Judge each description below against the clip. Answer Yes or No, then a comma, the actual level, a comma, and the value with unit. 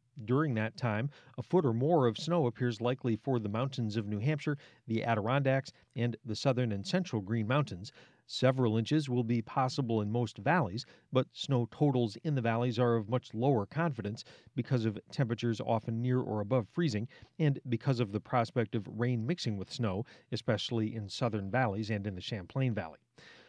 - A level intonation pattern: No, average, 3.0 semitones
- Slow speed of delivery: No, average, 185 wpm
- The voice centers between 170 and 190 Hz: No, low, 120 Hz